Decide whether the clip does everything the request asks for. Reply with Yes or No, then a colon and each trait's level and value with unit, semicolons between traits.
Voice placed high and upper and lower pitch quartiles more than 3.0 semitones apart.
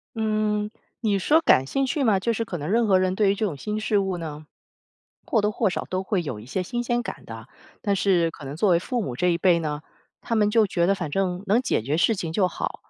Yes: high, 195 Hz; average, 4.2 semitones